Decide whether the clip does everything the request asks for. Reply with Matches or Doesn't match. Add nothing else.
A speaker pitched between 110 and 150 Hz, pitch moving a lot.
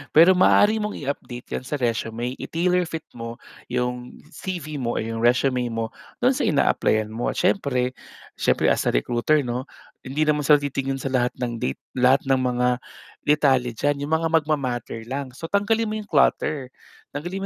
Doesn't match